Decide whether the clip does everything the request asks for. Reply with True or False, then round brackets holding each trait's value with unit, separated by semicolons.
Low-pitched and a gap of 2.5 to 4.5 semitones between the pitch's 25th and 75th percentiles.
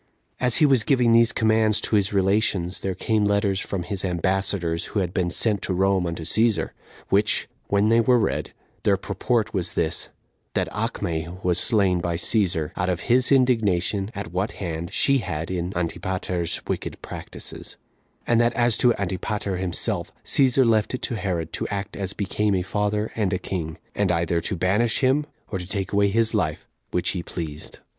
True (100 Hz; 3.8 semitones)